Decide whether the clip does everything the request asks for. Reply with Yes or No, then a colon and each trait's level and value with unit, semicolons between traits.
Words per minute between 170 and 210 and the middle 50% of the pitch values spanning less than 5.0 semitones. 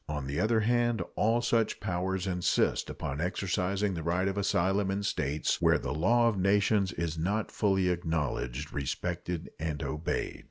No: average, 160 wpm; average, 3.8 semitones